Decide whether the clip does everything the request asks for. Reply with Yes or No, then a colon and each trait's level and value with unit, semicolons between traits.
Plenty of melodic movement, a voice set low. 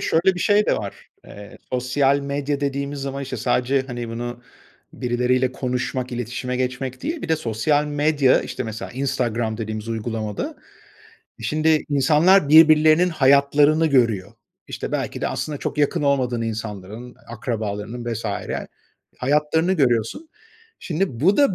No: average, 4.1 semitones; low, 130 Hz